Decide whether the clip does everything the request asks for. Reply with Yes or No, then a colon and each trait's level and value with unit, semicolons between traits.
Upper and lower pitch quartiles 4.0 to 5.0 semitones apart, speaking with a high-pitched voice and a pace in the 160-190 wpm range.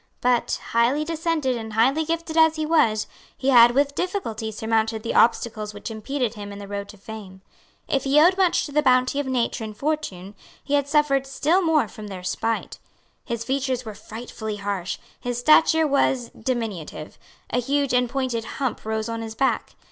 Yes: average, 4.6 semitones; high, 245 Hz; average, 185 wpm